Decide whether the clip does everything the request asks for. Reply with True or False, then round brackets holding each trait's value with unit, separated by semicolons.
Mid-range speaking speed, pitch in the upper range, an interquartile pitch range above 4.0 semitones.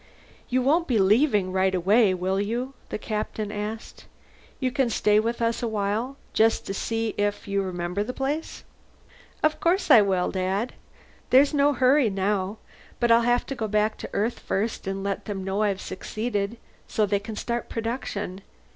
False (175 wpm; 215 Hz; 3.5 semitones)